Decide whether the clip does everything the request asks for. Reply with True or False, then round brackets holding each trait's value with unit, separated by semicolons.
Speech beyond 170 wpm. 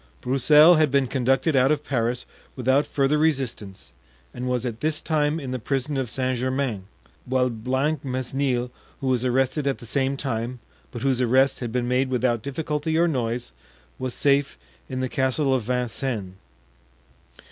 False (160 wpm)